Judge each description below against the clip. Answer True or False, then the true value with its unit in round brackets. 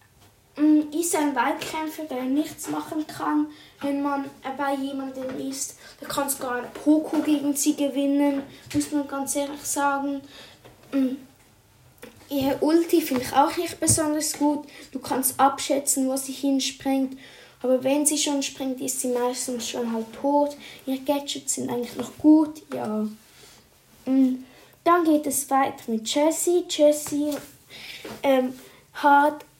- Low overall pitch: False (280 Hz)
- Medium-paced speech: True (135 wpm)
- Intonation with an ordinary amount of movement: False (2.0 semitones)